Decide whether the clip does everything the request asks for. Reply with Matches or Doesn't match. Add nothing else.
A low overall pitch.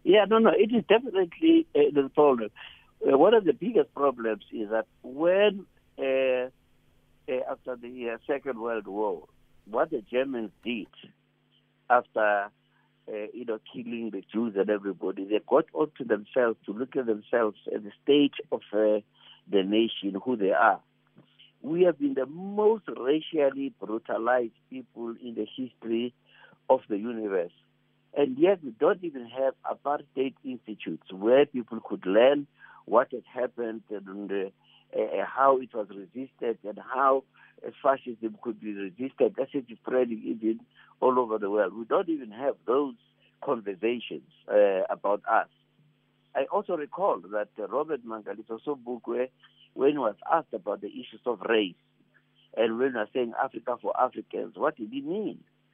Matches